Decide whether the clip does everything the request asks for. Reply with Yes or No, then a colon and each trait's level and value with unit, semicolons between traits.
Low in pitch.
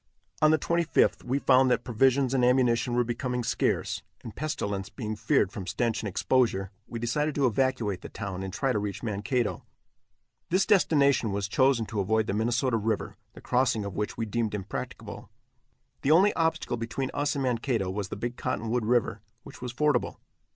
Yes: low, 120 Hz